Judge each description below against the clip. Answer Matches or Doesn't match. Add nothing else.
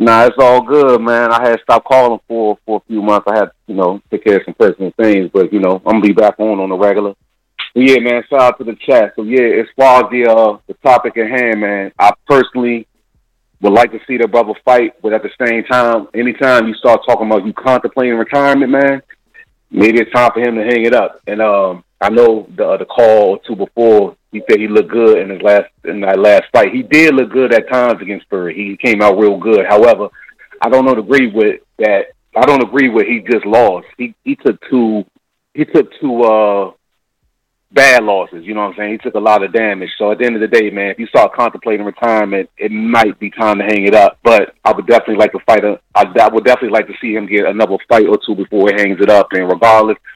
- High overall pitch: Doesn't match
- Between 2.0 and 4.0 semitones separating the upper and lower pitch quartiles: Matches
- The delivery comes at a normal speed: Doesn't match